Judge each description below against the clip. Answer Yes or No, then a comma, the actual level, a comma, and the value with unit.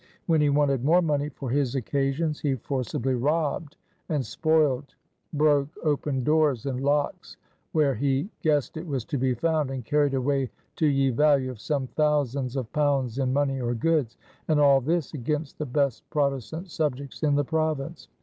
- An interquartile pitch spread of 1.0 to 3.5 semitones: Yes, narrow, 2.4 semitones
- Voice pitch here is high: No, medium, 140 Hz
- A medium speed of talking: Yes, average, 170 wpm